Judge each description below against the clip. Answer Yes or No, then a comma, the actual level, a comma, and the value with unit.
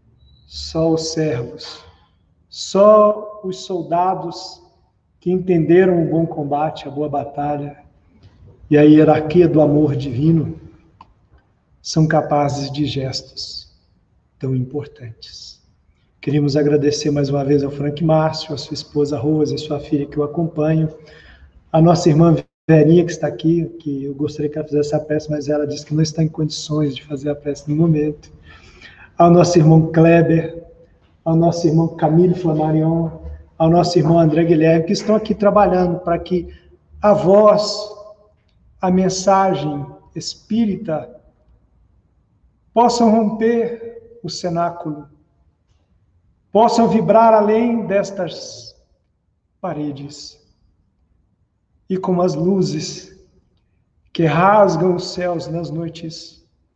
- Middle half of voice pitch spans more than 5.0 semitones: No, average, 3.6 semitones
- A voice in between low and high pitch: Yes, medium, 155 Hz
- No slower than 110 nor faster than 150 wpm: Yes, average, 125 wpm